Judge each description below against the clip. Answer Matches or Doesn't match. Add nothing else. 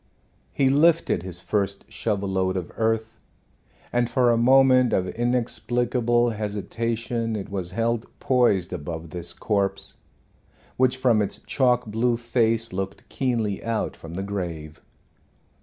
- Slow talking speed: Matches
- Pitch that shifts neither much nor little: Matches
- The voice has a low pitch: Matches